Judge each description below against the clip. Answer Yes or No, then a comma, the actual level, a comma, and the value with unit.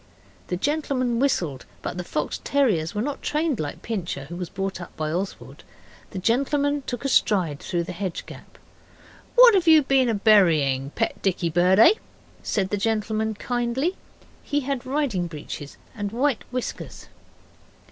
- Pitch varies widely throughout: Yes, wide, 7.5 semitones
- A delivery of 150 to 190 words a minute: Yes, average, 155 wpm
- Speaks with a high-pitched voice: Yes, high, 215 Hz